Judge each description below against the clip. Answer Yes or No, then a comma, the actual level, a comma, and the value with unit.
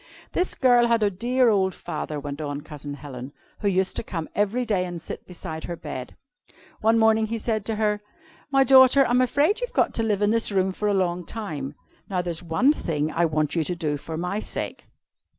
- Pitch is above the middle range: Yes, high, 195 Hz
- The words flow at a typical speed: No, fast, 215 wpm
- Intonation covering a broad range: Yes, wide, 6.1 semitones